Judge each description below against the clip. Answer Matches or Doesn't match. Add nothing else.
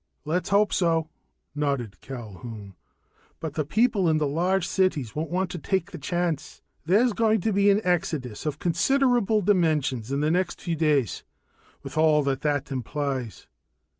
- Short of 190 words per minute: Matches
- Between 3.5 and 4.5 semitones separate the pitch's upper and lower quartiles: Doesn't match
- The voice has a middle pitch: Matches